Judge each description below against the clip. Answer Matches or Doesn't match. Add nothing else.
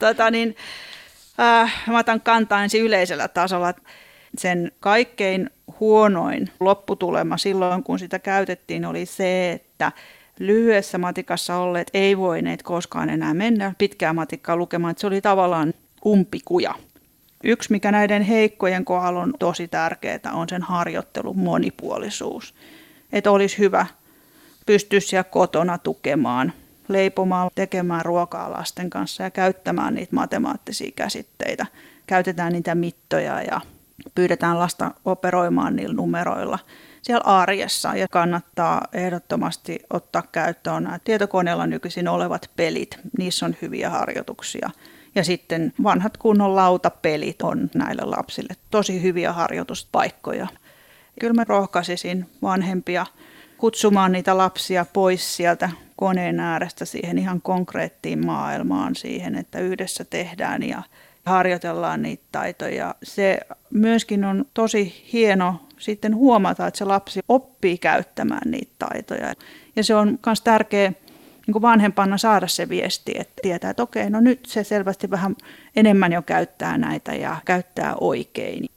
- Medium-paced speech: Matches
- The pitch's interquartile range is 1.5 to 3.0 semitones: Doesn't match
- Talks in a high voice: Matches